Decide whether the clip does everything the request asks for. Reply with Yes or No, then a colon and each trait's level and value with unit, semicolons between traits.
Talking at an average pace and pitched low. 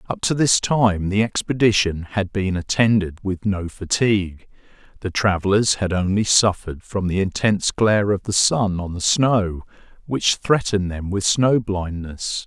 Yes: average, 160 wpm; low, 100 Hz